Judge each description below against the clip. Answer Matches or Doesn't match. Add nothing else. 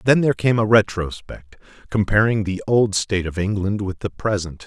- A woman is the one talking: Doesn't match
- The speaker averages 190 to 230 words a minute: Doesn't match